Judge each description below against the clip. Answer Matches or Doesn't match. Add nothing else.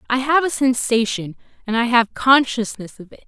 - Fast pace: Doesn't match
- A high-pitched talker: Matches